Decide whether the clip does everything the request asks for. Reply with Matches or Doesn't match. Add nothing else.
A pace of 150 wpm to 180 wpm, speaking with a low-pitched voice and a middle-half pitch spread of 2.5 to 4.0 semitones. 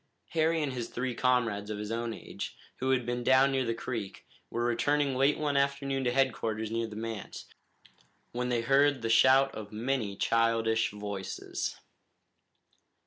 Matches